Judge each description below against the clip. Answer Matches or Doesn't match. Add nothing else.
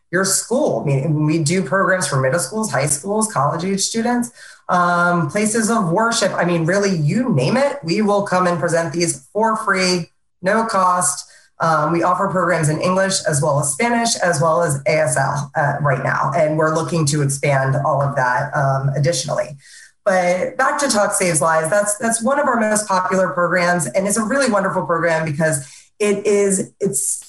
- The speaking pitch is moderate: Matches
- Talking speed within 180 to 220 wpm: Matches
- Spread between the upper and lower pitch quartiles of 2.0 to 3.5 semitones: Doesn't match